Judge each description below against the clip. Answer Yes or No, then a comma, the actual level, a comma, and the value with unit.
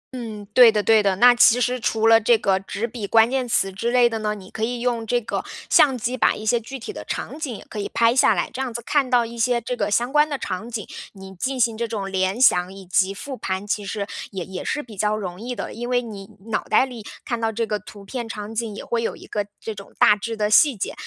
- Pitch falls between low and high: No, high, 225 Hz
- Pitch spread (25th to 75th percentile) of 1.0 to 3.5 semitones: Yes, average, 2.9 semitones